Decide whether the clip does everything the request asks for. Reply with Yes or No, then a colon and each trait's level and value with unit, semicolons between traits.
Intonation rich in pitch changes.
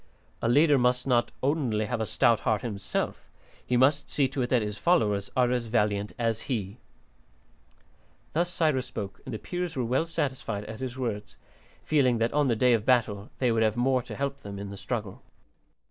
No: average, 3.7 semitones